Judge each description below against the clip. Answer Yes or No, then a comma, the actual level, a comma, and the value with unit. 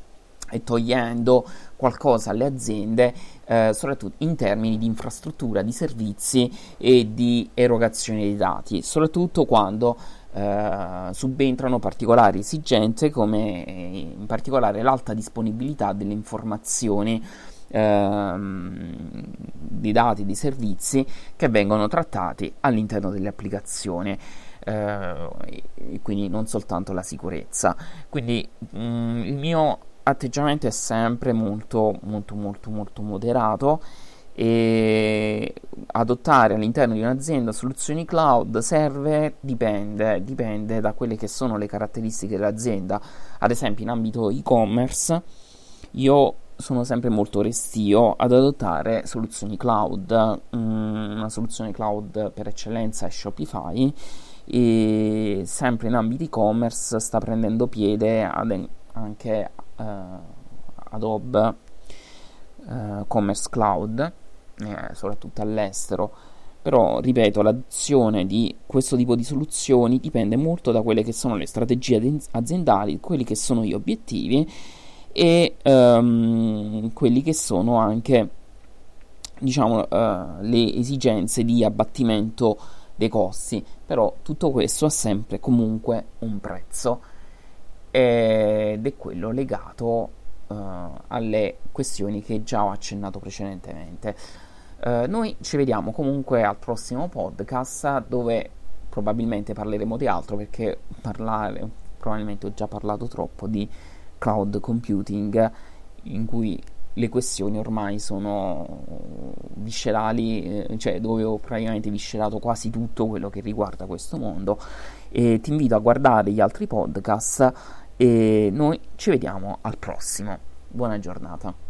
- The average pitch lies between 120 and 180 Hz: No, low, 110 Hz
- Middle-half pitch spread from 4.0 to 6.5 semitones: No, average, 3.0 semitones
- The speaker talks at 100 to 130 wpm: Yes, slow, 115 wpm